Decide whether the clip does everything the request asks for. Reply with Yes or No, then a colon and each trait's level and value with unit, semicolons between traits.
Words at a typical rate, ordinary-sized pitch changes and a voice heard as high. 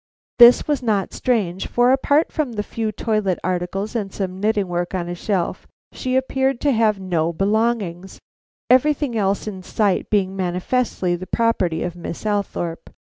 Yes: average, 160 wpm; average, 4.5 semitones; high, 205 Hz